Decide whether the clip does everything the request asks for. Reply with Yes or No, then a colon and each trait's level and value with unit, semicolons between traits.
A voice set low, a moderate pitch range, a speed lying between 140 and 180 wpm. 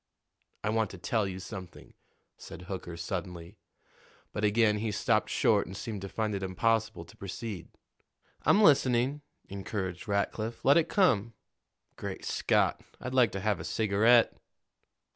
Yes: low, 105 Hz; average, 3.2 semitones; average, 145 wpm